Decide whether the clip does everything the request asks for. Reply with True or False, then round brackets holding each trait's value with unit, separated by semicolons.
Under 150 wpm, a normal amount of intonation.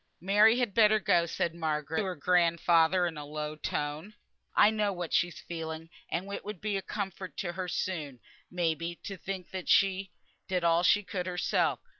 False (185 wpm; 3.1 semitones)